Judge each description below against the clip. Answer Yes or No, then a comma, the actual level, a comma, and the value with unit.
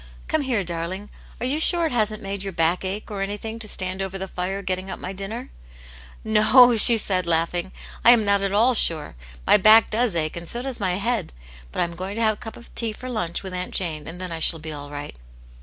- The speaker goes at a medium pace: No, fast, 255 wpm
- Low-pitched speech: No, high, 195 Hz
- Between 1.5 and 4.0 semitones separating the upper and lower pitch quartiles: No, average, 4.4 semitones